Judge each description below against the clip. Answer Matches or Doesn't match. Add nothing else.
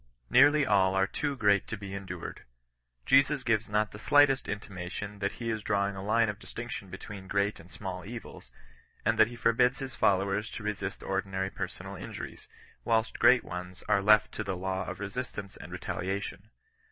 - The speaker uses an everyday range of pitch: Matches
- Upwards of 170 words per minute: Matches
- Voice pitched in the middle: Doesn't match